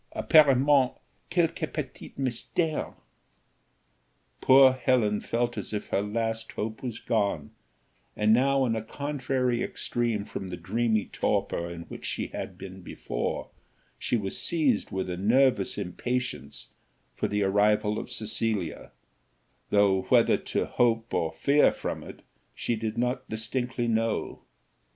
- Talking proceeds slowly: Yes, slow, 130 wpm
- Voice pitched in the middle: No, low, 115 Hz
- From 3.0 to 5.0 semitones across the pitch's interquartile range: Yes, average, 3.9 semitones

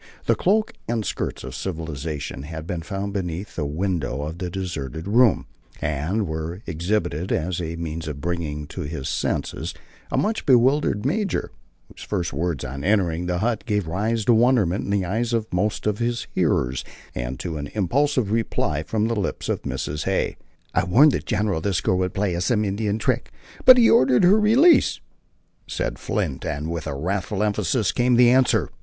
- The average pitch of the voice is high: No, very low, 95 Hz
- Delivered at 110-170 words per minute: No, average, 180 wpm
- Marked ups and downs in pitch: Yes, wide, 5.9 semitones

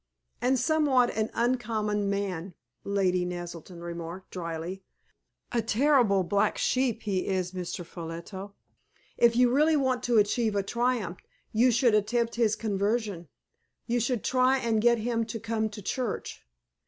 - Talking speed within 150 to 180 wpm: No, average, 140 wpm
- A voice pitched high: Yes, high, 215 Hz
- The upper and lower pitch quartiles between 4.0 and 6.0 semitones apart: Yes, average, 4.3 semitones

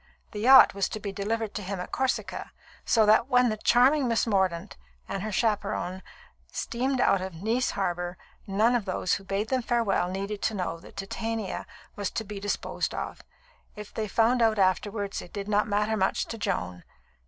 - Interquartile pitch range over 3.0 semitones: No, average, 2.7 semitones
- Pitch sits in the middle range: No, high, 210 Hz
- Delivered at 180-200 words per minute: Yes, average, 190 wpm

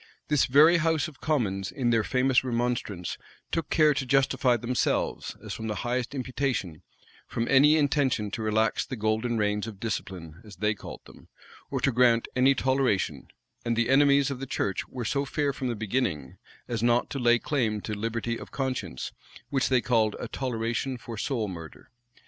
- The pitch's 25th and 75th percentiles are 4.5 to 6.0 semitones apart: No, average, 3.7 semitones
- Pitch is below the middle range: Yes, low, 120 Hz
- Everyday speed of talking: Yes, average, 180 wpm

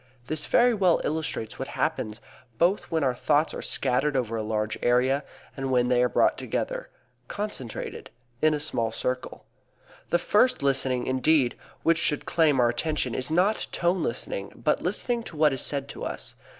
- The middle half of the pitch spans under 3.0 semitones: No, average, 4.7 semitones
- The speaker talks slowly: No, average, 175 wpm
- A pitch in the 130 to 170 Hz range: Yes, medium, 140 Hz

